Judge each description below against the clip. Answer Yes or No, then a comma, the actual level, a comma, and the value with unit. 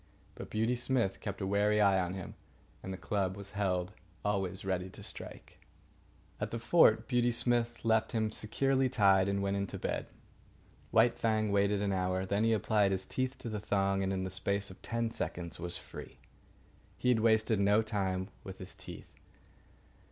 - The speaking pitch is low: Yes, low, 100 Hz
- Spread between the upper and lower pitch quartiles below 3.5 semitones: Yes, average, 2.8 semitones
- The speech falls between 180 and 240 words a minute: Yes, average, 185 wpm